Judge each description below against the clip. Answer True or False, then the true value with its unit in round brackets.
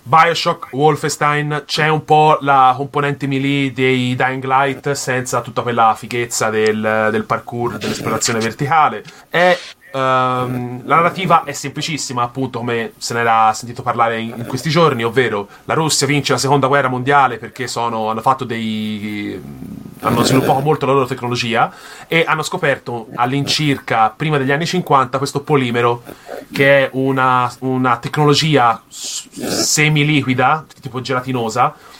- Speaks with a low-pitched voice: True (130 Hz)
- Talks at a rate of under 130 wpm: False (135 wpm)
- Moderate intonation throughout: True (3.3 semitones)